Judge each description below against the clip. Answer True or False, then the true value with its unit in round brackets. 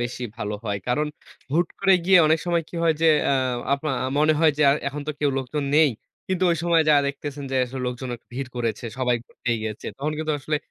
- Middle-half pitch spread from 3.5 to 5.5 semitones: True (4.1 semitones)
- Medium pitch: True (145 Hz)